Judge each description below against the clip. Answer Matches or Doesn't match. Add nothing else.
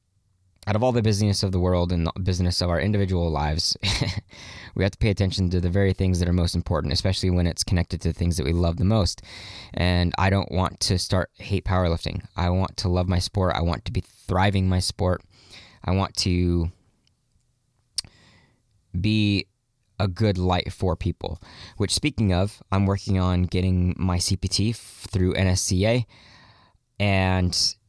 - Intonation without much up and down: Matches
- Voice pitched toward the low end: Matches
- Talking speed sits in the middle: Matches